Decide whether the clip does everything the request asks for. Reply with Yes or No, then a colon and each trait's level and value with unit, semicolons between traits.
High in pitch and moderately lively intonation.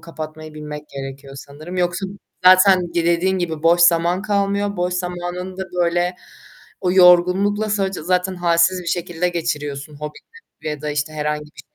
No: medium, 175 Hz; average, 3.0 semitones